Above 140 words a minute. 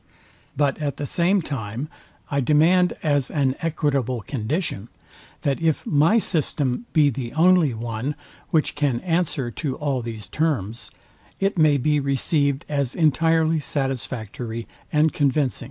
No: slow, 135 wpm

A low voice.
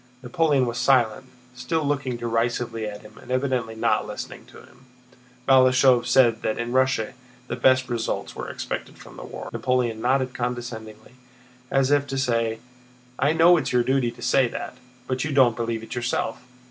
Yes: low, 125 Hz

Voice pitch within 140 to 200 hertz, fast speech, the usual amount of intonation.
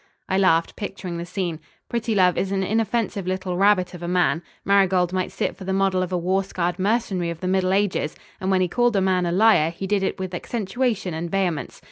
No: medium, 185 Hz; fast, 220 wpm; narrow, 1.7 semitones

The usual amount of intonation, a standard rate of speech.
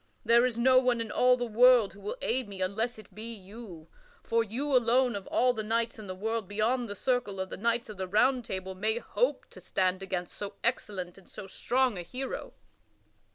No: average, 3.9 semitones; fast, 215 wpm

